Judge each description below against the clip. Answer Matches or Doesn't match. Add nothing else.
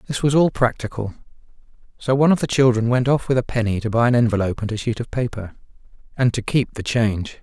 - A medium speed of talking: Doesn't match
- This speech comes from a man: Matches